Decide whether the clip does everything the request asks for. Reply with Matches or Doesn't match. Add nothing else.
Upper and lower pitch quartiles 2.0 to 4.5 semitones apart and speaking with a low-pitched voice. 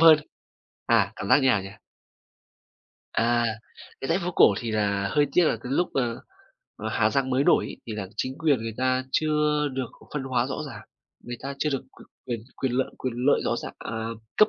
Matches